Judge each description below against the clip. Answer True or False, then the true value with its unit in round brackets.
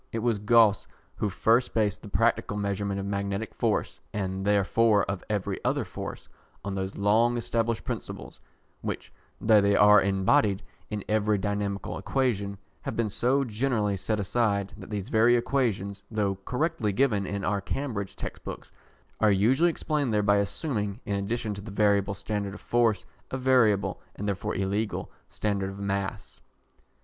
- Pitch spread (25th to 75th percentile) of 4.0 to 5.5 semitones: False (2.4 semitones)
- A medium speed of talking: True (160 wpm)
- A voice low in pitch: True (105 Hz)